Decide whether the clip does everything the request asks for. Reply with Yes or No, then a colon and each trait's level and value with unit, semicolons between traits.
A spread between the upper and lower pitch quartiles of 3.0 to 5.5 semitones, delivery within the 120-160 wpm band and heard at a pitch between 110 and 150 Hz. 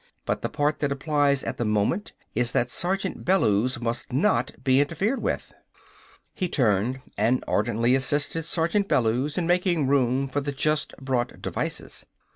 Yes: average, 4.9 semitones; average, 155 wpm; medium, 140 Hz